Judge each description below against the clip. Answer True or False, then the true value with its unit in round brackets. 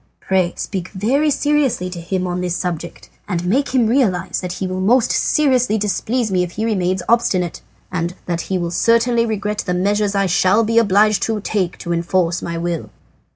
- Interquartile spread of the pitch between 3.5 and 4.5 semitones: True (4.1 semitones)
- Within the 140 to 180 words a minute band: False (190 wpm)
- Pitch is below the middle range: False (190 Hz)